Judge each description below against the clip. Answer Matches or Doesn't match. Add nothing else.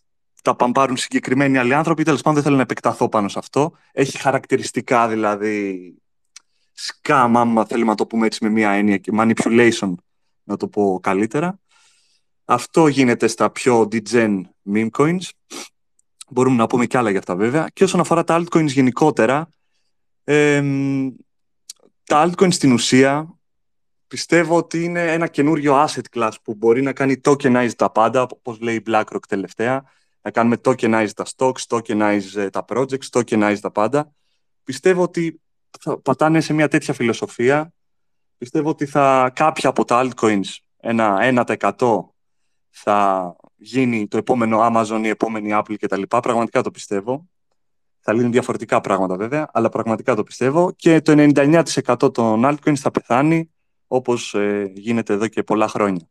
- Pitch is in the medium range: Doesn't match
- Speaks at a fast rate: Doesn't match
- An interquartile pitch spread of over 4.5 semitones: Matches